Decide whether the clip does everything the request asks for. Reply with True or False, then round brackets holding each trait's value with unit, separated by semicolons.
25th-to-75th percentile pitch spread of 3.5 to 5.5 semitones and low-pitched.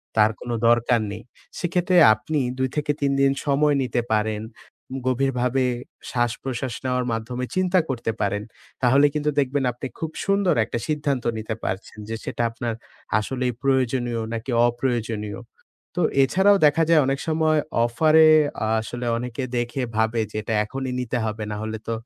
True (3.8 semitones; 125 Hz)